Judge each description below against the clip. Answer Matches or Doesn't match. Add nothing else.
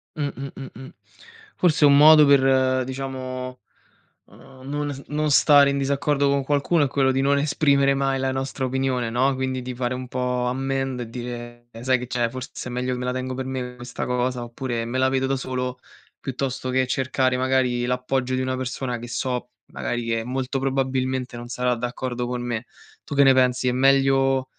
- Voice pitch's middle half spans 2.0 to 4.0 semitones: Doesn't match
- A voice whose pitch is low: Matches